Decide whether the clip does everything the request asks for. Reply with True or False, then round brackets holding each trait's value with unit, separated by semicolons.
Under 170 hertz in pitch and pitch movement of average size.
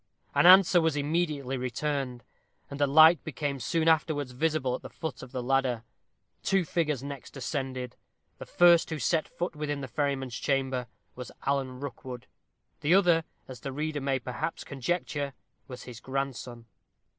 True (140 Hz; 3.5 semitones)